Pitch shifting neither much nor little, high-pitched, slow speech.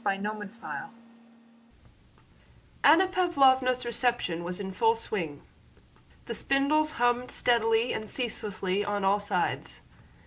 Yes: average, 4.0 semitones; high, 225 Hz; slow, 105 wpm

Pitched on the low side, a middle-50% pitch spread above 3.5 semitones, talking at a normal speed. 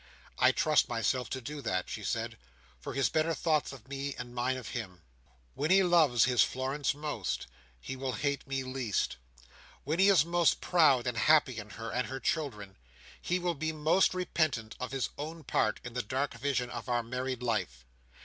Yes: low, 130 Hz; average, 4.1 semitones; average, 190 wpm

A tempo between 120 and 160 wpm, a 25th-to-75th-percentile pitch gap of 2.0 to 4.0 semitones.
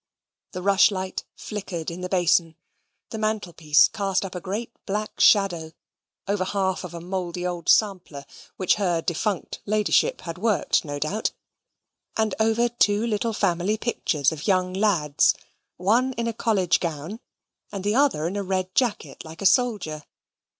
Yes: average, 155 wpm; average, 3.6 semitones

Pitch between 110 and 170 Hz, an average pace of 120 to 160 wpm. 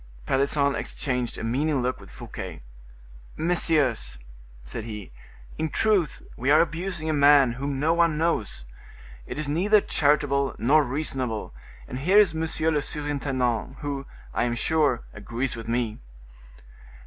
Yes: medium, 140 Hz; average, 140 wpm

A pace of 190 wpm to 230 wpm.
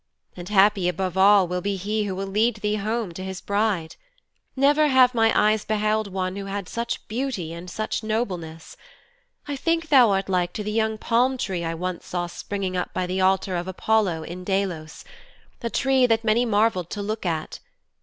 Yes: average, 200 wpm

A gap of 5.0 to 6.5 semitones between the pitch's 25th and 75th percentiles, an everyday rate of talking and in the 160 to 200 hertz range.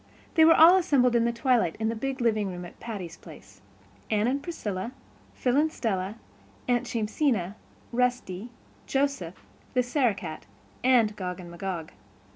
No: wide, 5.6 semitones; average, 145 wpm; high, 225 Hz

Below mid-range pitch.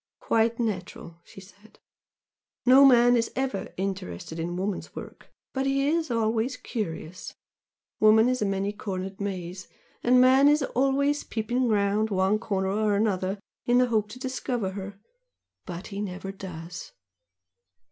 No: high, 210 Hz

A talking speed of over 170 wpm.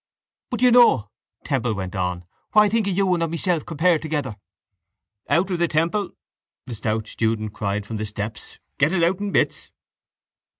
Yes: average, 185 wpm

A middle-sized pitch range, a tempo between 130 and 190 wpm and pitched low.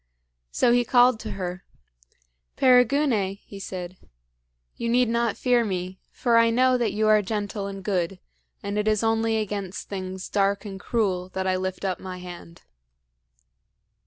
No: average, 3.6 semitones; average, 160 wpm; high, 205 Hz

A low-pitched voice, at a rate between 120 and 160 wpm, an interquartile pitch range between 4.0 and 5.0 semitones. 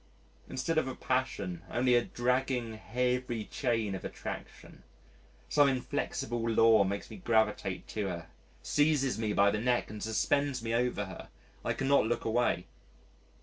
No: low, 120 Hz; average, 150 wpm; average, 3.3 semitones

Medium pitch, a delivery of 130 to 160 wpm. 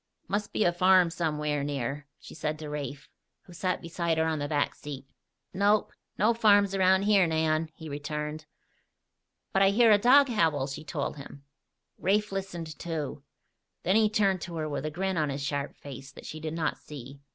No: medium, 160 Hz; average, 190 wpm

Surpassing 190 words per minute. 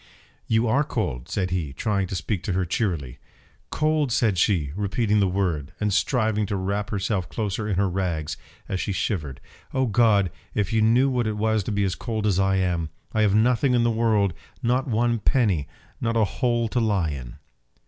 Yes: average, 200 wpm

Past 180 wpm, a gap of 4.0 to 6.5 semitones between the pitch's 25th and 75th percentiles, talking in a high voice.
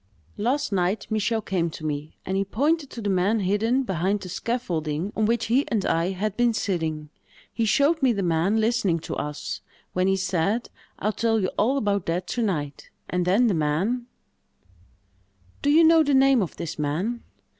Yes: average, 190 wpm; average, 5.1 semitones; high, 205 Hz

